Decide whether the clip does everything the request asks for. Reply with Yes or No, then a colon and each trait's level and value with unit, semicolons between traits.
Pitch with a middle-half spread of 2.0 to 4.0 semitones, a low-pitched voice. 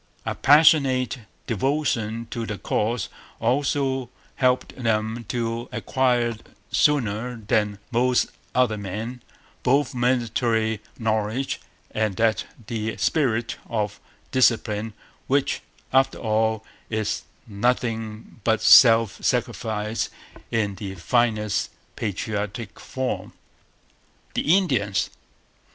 Yes: average, 2.8 semitones; low, 115 Hz